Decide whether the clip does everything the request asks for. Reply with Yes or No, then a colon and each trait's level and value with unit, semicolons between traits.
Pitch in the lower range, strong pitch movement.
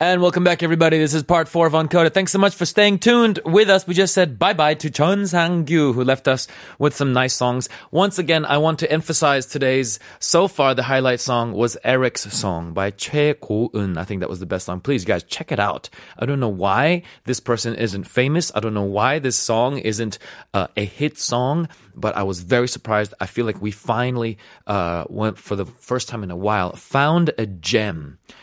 Yes: low, 130 Hz; wide, 7.1 semitones